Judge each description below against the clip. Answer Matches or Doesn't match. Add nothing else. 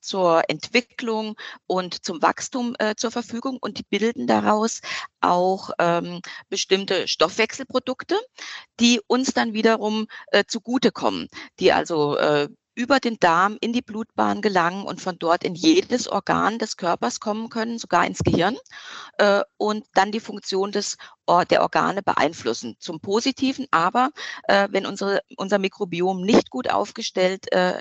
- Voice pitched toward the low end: Doesn't match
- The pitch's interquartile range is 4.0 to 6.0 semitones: Matches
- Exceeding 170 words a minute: Doesn't match